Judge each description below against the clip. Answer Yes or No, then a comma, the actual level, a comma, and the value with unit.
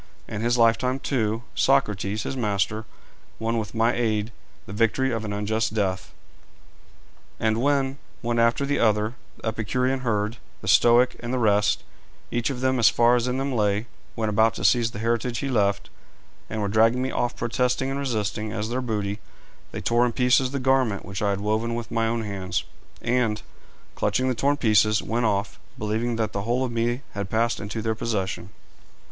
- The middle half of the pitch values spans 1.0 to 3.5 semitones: Yes, average, 2.7 semitones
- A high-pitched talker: No, low, 115 Hz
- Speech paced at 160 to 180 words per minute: No, average, 190 wpm